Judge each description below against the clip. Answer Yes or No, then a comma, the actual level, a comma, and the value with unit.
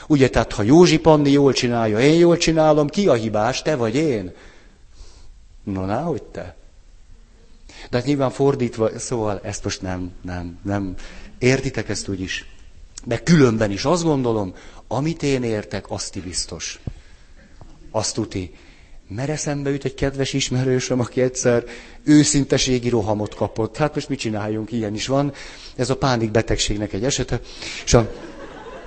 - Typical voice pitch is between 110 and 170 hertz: Yes, low, 120 Hz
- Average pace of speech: Yes, average, 145 wpm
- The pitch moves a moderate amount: Yes, average, 4.8 semitones